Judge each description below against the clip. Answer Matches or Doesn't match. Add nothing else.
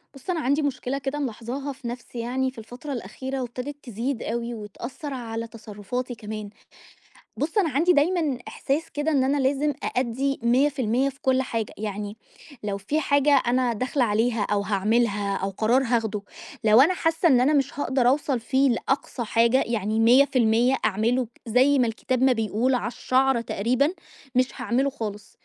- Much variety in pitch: Doesn't match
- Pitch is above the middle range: Matches